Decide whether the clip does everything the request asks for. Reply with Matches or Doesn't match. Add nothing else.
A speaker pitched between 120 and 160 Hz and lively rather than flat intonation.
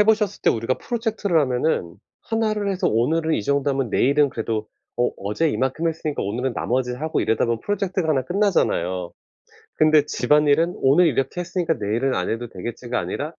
Matches